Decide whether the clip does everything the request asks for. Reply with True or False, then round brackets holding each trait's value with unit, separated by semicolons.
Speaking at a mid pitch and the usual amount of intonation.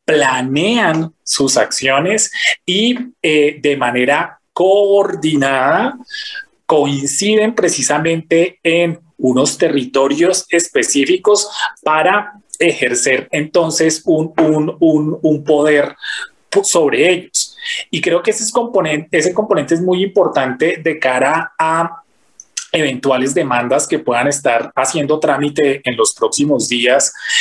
False (165 Hz; 6.1 semitones)